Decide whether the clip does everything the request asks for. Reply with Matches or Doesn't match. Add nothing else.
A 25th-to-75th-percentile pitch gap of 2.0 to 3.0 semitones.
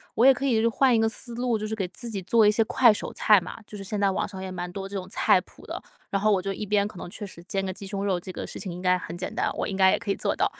Matches